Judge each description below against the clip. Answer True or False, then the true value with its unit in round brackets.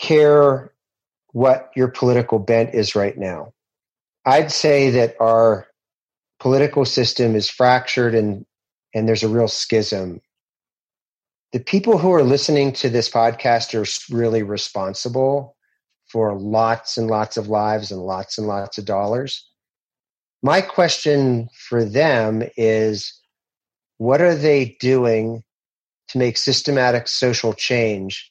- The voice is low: True (115 Hz)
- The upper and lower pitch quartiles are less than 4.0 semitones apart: True (3.1 semitones)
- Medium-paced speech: False (125 wpm)